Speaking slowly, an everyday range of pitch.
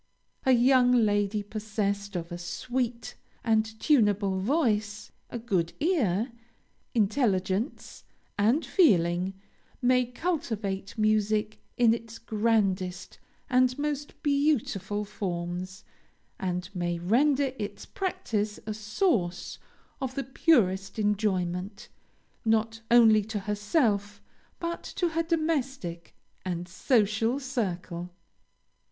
Yes: slow, 100 wpm; average, 4.5 semitones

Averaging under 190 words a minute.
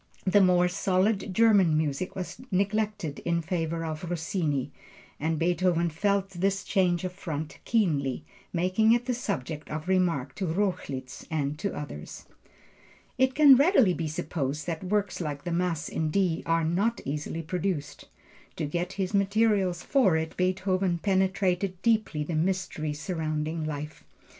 Yes: average, 145 wpm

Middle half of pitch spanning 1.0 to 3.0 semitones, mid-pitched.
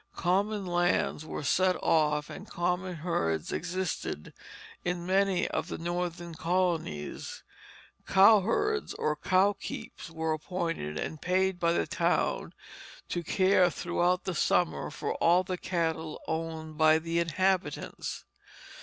Yes: narrow, 2.5 semitones; medium, 175 Hz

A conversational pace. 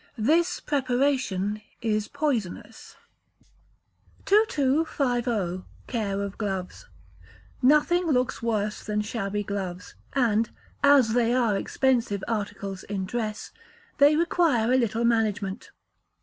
No: slow, 100 wpm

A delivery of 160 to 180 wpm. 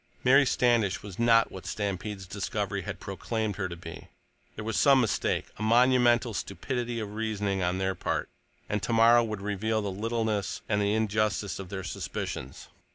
Yes: average, 165 wpm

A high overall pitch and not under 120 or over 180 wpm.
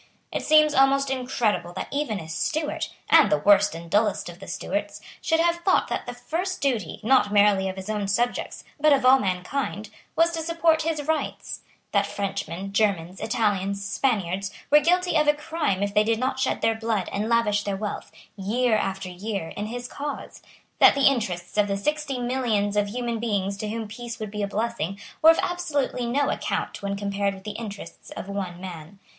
No: high, 215 Hz; average, 195 wpm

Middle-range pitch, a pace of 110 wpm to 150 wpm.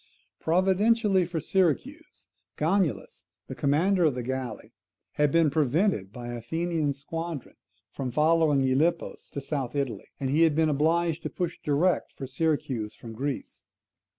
Yes: medium, 155 Hz; average, 145 wpm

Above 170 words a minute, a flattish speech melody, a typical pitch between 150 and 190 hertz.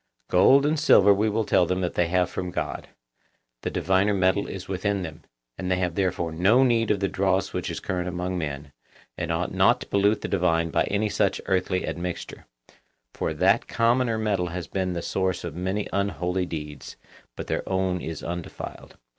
No: average, 190 wpm; narrow, 2.2 semitones; very low, 95 Hz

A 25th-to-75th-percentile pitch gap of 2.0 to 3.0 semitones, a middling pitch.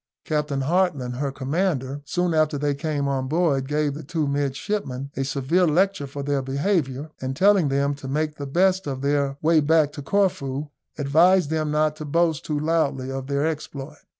Yes: average, 2.7 semitones; medium, 145 Hz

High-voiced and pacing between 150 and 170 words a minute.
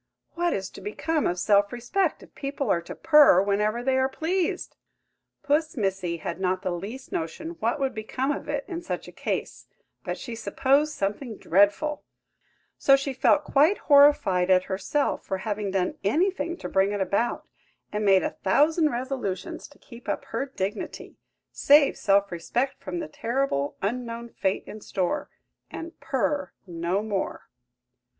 Yes: high, 235 Hz; average, 160 wpm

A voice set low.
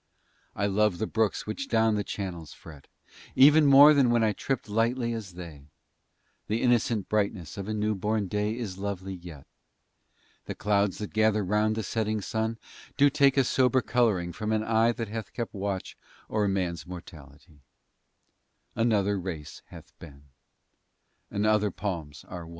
Yes: low, 105 Hz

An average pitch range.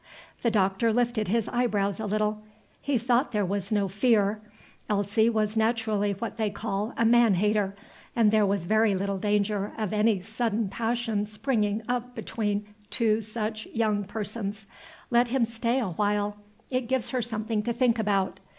No: narrow, 2.2 semitones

